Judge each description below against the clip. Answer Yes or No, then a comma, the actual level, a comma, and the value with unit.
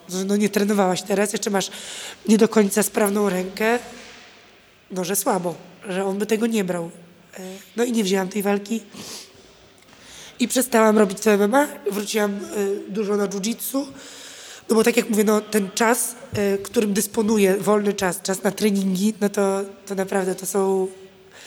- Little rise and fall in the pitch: Yes, narrow, 2.3 semitones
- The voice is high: Yes, high, 205 Hz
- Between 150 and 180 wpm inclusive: Yes, average, 155 wpm